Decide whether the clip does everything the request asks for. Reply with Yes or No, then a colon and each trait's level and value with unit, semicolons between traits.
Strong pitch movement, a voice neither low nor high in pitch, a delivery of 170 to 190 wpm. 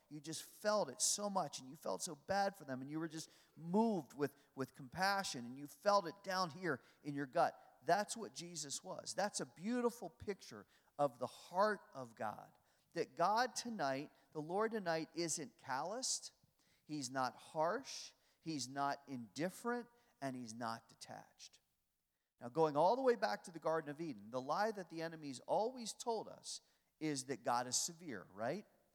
Yes: wide, 6.4 semitones; medium, 160 Hz; average, 180 wpm